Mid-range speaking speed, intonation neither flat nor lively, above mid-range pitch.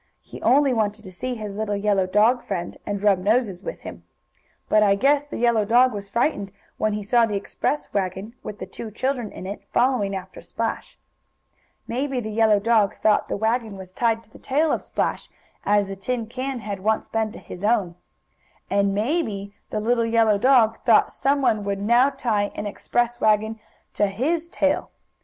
Yes: average, 195 wpm; average, 3.2 semitones; high, 220 Hz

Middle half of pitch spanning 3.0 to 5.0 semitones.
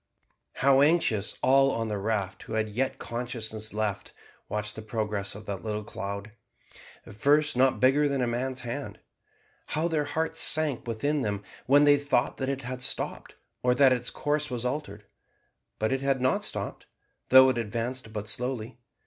Yes: average, 4.0 semitones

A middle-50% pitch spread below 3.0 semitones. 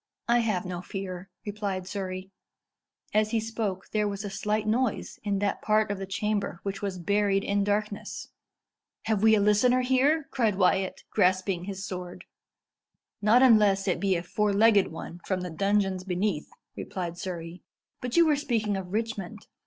Yes: narrow, 2.4 semitones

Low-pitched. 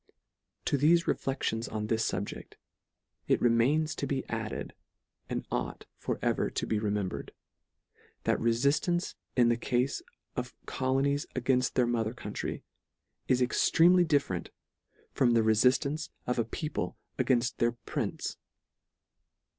Yes: low, 125 Hz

